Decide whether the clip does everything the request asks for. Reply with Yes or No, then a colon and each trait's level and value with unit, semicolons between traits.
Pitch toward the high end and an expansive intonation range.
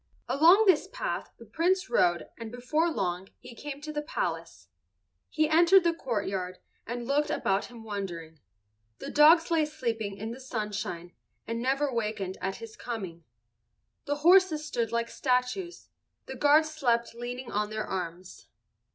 Yes: high, 245 Hz; wide, 6.5 semitones